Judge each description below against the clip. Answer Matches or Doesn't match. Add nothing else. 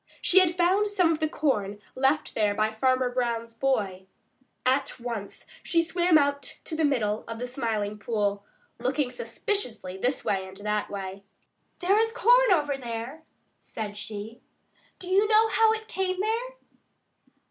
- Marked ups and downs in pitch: Matches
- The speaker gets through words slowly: Doesn't match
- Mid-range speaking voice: Doesn't match